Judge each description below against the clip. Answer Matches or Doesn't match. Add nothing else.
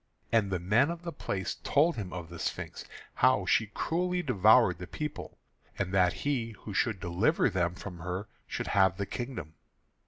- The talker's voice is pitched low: Matches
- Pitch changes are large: Matches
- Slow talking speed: Doesn't match